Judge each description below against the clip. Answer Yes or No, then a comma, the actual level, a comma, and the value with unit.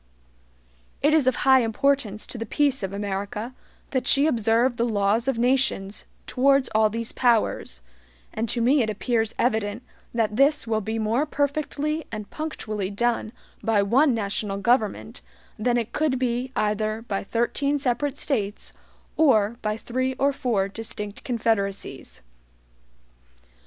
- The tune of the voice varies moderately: Yes, average, 3.7 semitones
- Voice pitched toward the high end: Yes, high, 230 Hz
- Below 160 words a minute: Yes, average, 140 wpm